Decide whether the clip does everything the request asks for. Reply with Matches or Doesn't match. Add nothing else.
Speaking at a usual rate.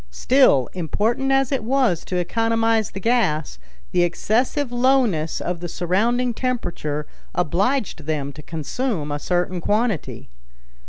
Doesn't match